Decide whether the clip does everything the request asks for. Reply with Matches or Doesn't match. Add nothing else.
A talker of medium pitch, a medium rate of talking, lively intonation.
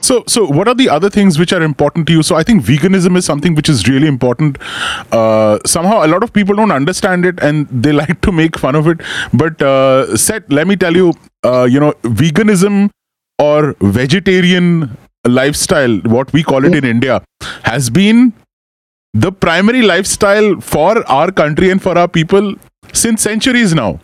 Matches